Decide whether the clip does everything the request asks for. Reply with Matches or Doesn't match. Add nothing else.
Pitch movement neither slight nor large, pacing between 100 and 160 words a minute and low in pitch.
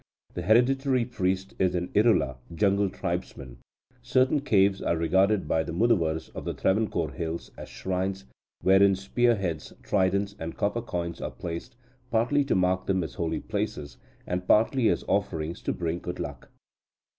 Matches